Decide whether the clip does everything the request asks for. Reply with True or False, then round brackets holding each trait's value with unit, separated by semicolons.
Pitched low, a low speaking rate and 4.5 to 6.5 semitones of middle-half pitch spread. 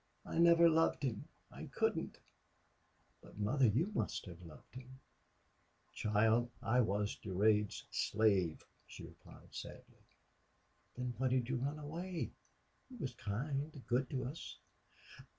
True (125 Hz; 130 wpm; 5.5 semitones)